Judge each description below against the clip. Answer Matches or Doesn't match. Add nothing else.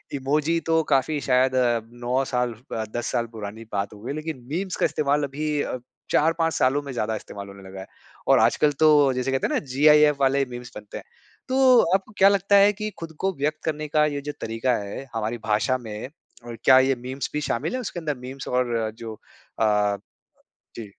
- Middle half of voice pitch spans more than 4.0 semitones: Matches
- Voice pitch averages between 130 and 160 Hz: Matches